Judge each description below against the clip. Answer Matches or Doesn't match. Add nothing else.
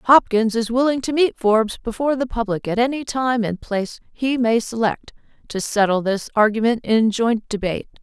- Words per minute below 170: Doesn't match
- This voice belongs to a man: Doesn't match